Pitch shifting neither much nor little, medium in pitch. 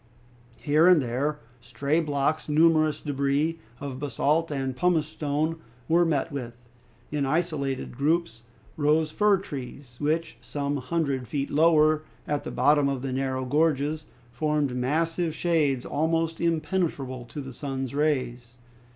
Yes: average, 3.0 semitones; medium, 145 Hz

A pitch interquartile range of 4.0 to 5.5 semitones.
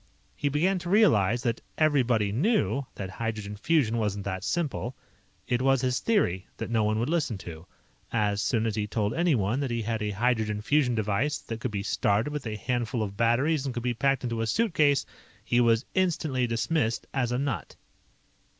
Yes: average, 4.7 semitones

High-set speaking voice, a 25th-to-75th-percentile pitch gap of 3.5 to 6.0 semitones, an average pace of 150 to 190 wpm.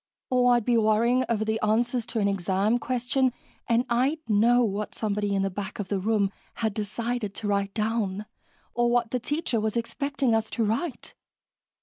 No: high, 225 Hz; average, 2.8 semitones; average, 185 wpm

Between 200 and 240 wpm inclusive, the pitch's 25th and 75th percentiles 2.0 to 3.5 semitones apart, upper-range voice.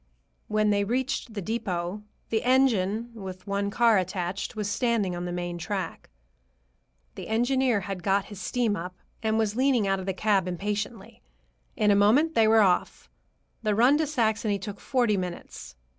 No: average, 170 wpm; average, 3.2 semitones; high, 210 Hz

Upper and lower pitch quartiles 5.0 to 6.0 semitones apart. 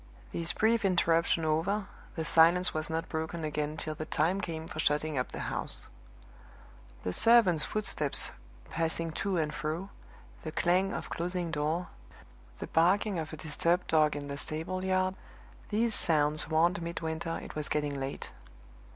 No: average, 2.8 semitones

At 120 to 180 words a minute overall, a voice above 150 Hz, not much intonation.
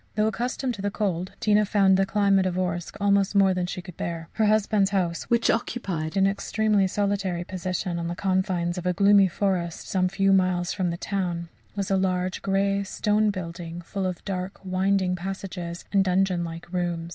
No: average, 190 wpm; high, 190 Hz; narrow, 2.1 semitones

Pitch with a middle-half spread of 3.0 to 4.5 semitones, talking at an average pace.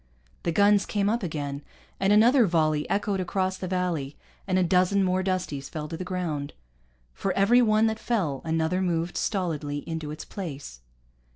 Yes: average, 4.1 semitones; average, 170 wpm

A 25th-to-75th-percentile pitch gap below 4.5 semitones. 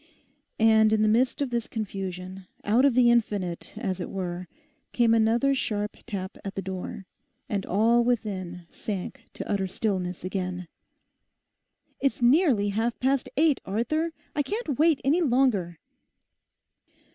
No: average, 4.8 semitones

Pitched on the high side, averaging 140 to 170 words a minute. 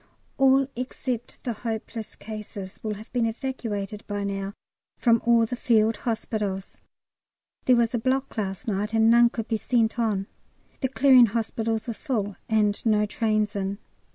Yes: high, 225 Hz; average, 155 wpm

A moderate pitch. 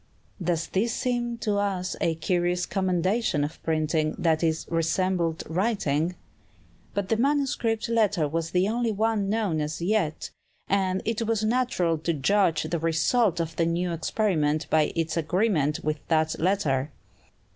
Yes: medium, 180 Hz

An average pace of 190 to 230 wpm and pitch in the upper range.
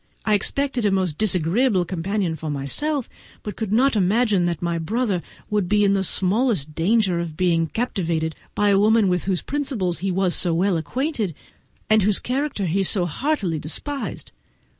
No: average, 170 wpm; high, 195 Hz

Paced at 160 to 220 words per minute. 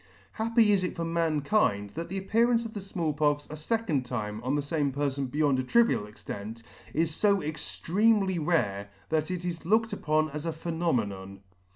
Yes: average, 180 wpm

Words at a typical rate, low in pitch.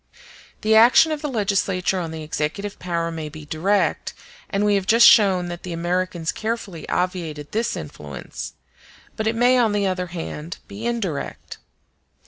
No: average, 160 wpm; medium, 185 Hz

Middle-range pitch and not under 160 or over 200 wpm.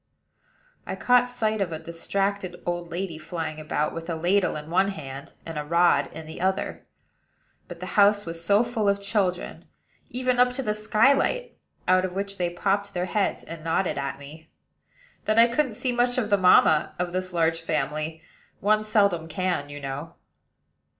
Yes: medium, 180 Hz; average, 180 wpm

